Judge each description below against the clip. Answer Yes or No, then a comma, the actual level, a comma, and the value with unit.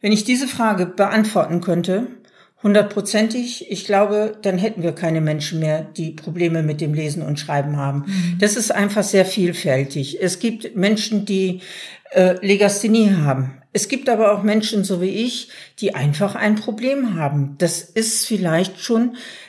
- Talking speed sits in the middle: Yes, average, 160 wpm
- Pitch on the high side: Yes, high, 200 Hz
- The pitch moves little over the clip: No, average, 4.4 semitones